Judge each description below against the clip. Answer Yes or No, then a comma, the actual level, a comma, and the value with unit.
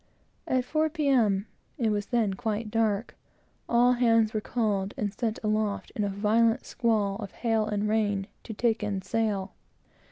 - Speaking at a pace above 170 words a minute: No, average, 165 wpm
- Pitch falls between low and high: No, high, 215 Hz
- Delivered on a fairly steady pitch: Yes, narrow, 2.1 semitones